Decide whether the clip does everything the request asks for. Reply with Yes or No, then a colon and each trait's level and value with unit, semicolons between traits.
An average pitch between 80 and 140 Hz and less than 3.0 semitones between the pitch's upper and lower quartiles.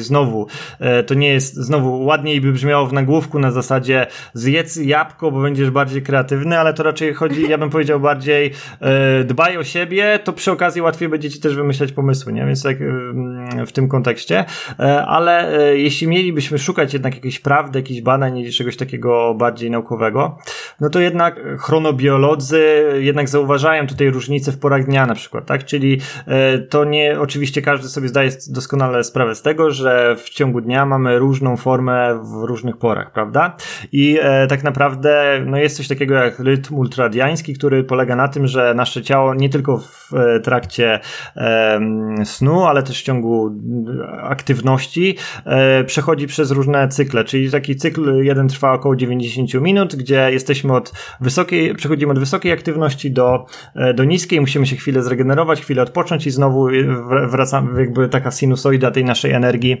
Yes: low, 135 Hz; narrow, 2.5 semitones